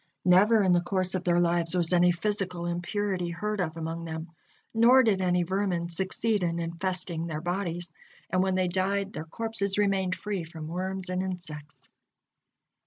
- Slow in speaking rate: No, average, 170 wpm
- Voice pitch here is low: No, medium, 180 Hz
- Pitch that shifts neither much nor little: No, narrow, 2.3 semitones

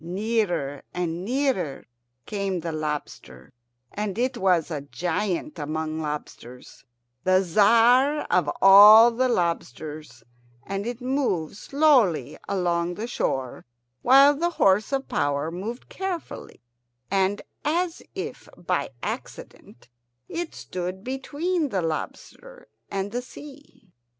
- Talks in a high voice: Yes, high, 195 Hz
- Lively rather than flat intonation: Yes, wide, 7.6 semitones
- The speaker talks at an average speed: No, slow, 115 wpm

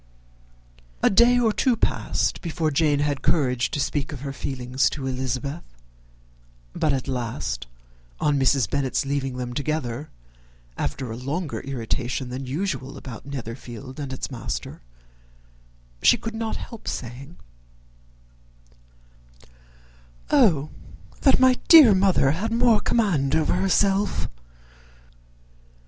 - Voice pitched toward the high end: No, medium, 140 Hz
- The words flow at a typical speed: No, slow, 120 wpm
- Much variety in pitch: Yes, wide, 5.7 semitones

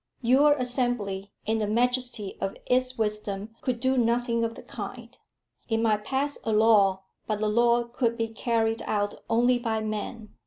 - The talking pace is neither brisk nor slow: Yes, average, 165 wpm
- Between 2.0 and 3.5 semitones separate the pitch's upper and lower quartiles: Yes, narrow, 2.4 semitones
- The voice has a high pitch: Yes, high, 230 Hz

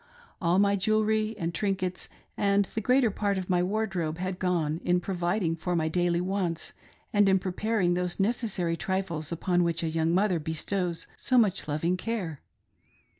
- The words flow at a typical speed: Yes, average, 165 wpm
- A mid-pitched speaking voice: Yes, medium, 180 Hz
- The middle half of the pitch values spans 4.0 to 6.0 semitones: No, average, 2.9 semitones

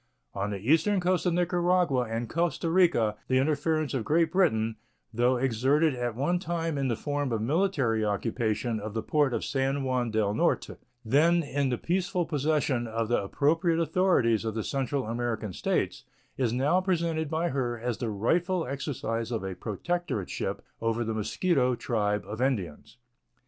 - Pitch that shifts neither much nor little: No, wide, 6.4 semitones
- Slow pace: No, average, 165 wpm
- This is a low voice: Yes, low, 130 Hz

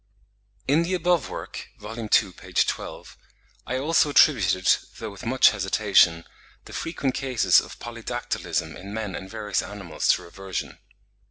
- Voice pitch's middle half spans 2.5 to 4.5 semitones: No, wide, 5.4 semitones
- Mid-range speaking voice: No, low, 110 Hz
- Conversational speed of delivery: Yes, average, 145 wpm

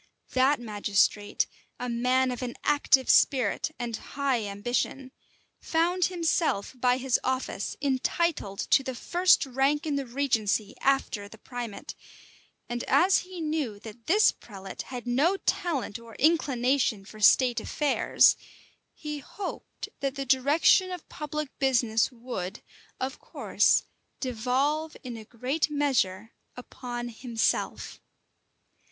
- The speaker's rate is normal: No, slow, 125 wpm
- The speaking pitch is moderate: No, very high, 255 Hz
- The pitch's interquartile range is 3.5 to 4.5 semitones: Yes, average, 3.9 semitones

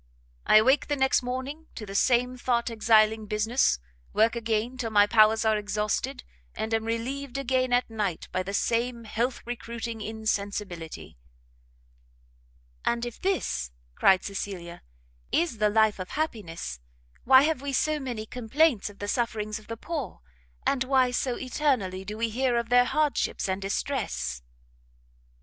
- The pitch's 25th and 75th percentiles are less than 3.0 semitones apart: No, average, 3.4 semitones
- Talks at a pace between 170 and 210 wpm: No, average, 150 wpm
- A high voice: Yes, high, 230 Hz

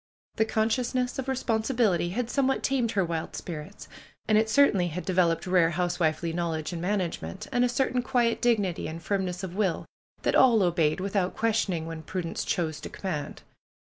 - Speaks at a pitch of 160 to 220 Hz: Yes, high, 190 Hz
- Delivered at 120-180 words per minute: Yes, average, 170 wpm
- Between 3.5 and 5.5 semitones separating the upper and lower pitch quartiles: Yes, average, 5.2 semitones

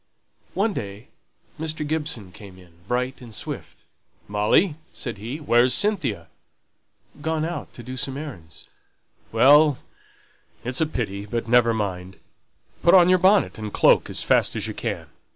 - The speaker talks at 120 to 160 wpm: Yes, average, 150 wpm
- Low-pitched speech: Yes, low, 125 Hz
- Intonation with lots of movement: Yes, wide, 6.8 semitones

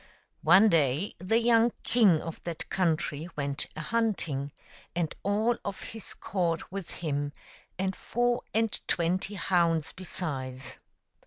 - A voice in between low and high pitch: Yes, medium, 175 Hz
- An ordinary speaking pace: No, slow, 130 wpm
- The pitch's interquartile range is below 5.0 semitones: No, average, 5.3 semitones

